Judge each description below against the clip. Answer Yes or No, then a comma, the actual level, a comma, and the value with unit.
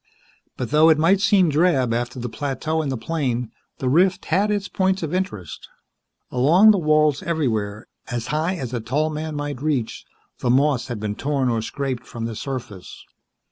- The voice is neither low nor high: Yes, medium, 145 Hz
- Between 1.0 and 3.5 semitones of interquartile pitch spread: No, average, 4.8 semitones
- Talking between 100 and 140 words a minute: No, average, 180 wpm